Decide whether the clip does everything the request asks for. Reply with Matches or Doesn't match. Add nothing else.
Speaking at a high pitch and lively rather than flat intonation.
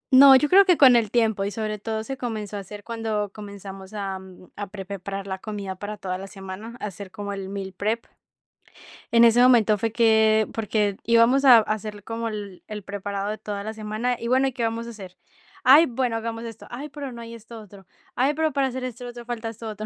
Doesn't match